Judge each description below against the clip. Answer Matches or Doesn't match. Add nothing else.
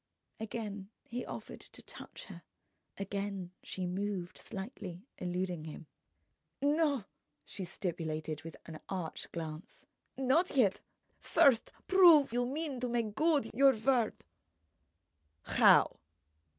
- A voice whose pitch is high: Matches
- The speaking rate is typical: Doesn't match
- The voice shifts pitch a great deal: Matches